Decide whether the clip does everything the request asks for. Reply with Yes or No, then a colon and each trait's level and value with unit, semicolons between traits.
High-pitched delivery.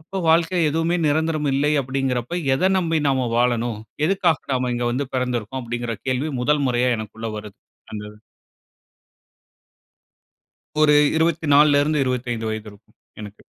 No: low, 130 Hz